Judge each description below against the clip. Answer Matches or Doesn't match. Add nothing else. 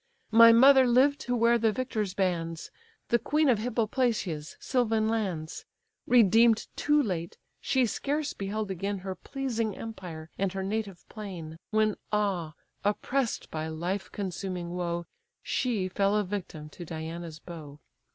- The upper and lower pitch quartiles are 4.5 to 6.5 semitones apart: Matches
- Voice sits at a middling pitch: Doesn't match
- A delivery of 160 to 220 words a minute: Doesn't match